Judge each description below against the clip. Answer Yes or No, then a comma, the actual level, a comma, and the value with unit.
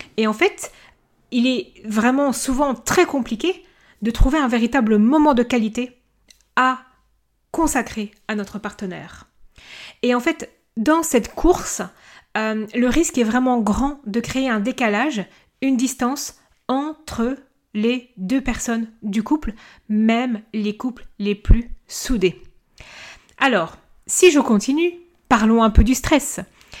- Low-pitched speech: No, high, 245 Hz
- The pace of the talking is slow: Yes, slow, 135 wpm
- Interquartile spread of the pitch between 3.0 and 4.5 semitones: Yes, average, 3.7 semitones